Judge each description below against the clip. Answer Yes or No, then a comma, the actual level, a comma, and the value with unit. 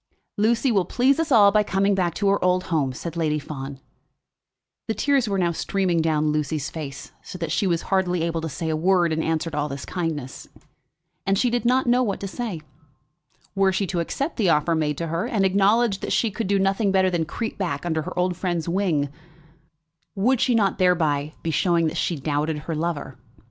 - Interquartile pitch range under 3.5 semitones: No, average, 4.1 semitones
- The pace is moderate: No, fast, 215 wpm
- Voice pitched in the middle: Yes, medium, 180 Hz